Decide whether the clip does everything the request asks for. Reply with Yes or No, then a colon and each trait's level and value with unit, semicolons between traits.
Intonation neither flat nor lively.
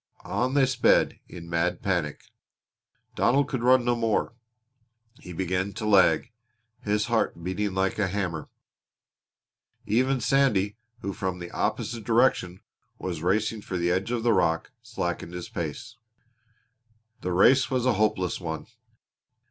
Yes: average, 4.8 semitones